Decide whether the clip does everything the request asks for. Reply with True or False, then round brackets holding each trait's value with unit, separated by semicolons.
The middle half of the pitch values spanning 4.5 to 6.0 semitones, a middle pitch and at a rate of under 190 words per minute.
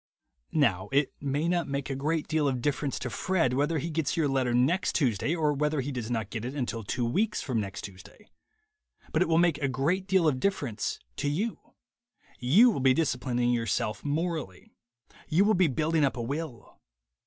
False (4.8 semitones; 145 Hz; 200 wpm)